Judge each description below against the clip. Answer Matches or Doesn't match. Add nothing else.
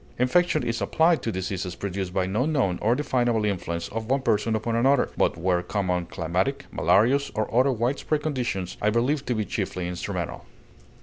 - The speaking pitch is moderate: Doesn't match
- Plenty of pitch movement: Matches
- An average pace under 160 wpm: Doesn't match